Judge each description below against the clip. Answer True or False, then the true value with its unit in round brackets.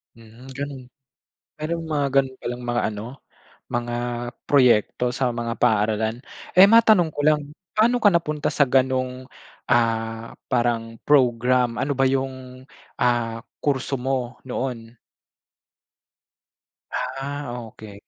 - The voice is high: False (125 Hz)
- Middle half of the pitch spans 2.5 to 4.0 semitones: True (3.0 semitones)